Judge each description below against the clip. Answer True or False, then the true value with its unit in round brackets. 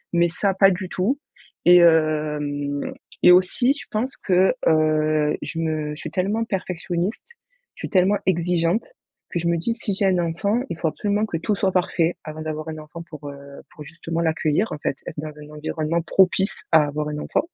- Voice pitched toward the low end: False (170 Hz)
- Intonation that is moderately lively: True (3.5 semitones)